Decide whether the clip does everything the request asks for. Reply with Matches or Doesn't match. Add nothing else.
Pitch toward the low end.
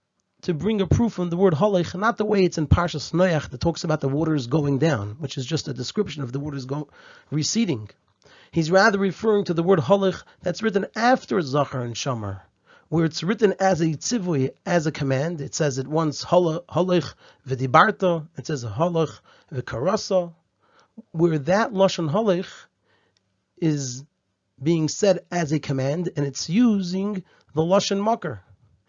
Doesn't match